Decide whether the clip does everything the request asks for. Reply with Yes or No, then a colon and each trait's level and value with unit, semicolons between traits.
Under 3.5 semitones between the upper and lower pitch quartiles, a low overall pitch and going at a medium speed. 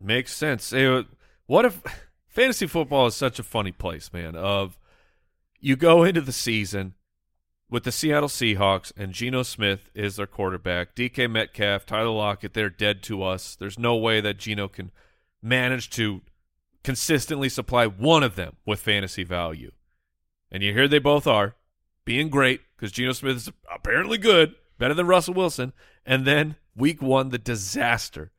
No: average, 5.2 semitones; low, 110 Hz; average, 160 wpm